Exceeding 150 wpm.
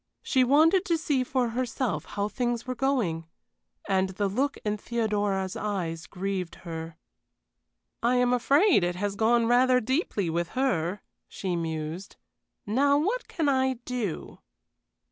No: average, 140 wpm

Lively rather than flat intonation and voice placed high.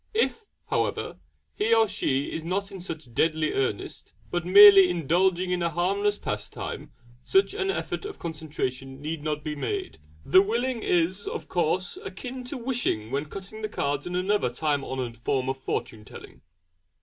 No: wide, 6.1 semitones; medium, 175 Hz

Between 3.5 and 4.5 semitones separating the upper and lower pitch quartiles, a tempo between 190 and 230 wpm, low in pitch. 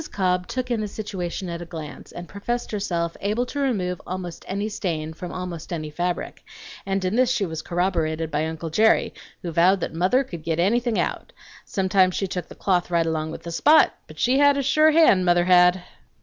No: average, 4.0 semitones; fast, 205 wpm; medium, 180 Hz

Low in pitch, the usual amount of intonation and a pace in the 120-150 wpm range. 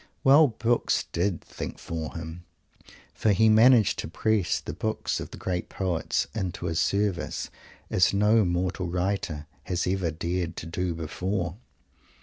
Yes: very low, 90 Hz; average, 3.5 semitones; average, 145 wpm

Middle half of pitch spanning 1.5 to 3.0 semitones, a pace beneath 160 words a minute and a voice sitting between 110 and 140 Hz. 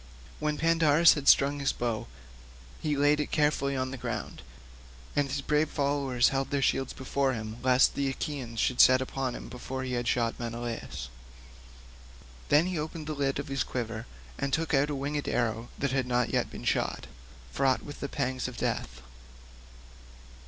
No: average, 2.7 semitones; average, 175 wpm; low, 135 Hz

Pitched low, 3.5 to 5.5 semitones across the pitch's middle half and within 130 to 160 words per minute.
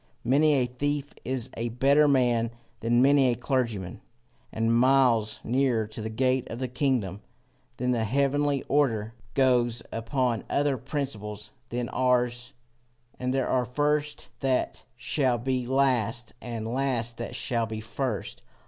No: low, 125 Hz; average, 2.8 semitones; average, 140 wpm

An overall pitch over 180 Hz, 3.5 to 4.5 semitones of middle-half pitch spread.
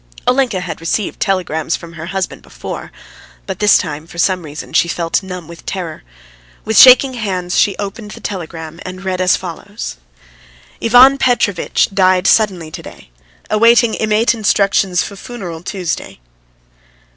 Yes: high, 190 Hz; average, 3.9 semitones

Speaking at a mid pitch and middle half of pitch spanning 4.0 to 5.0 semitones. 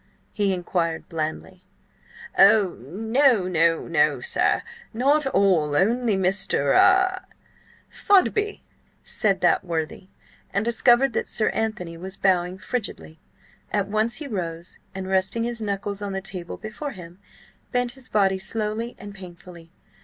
No: high, 195 Hz; average, 4.6 semitones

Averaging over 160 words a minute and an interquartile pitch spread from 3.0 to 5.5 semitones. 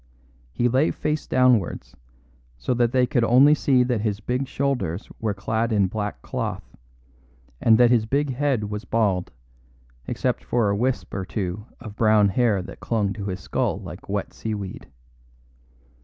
No: average, 155 wpm; average, 3.6 semitones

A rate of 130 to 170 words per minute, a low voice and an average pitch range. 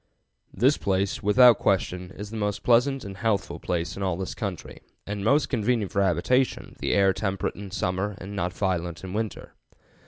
No: average, 180 wpm; low, 100 Hz; average, 3.0 semitones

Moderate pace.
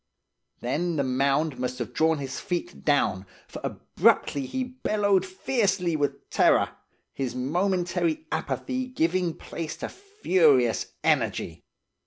No: slow, 120 wpm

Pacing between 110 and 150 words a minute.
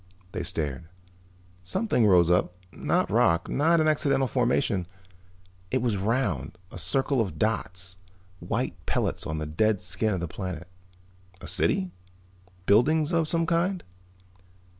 Yes: slow, 135 wpm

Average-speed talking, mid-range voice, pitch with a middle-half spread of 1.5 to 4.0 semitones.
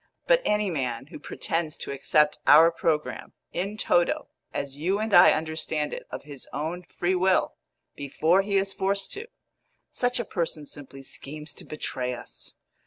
No: average, 165 wpm; medium, 165 Hz; average, 4.7 semitones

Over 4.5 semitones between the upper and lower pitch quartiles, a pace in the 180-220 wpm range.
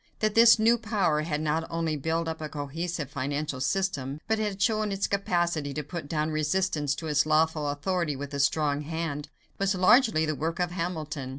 No: average, 4.0 semitones; average, 190 wpm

